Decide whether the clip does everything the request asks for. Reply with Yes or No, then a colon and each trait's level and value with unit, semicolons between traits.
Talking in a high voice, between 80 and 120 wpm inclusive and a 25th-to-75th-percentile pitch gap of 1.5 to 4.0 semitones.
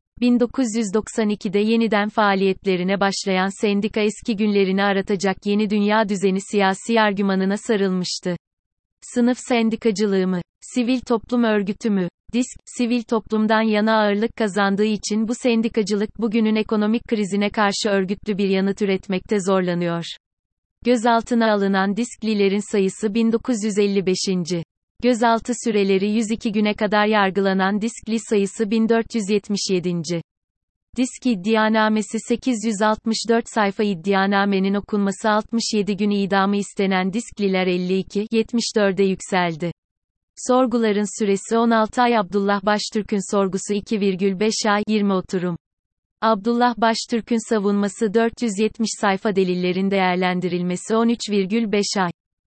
Yes: high, 210 Hz; average, 100 wpm; narrow, 2.5 semitones